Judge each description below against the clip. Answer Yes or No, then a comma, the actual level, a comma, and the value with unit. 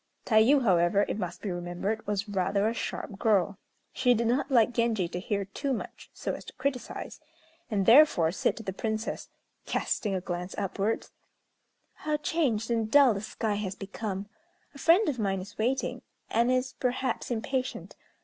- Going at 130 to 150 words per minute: No, average, 170 wpm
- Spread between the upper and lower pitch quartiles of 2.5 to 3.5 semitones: No, average, 4.3 semitones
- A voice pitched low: No, high, 220 Hz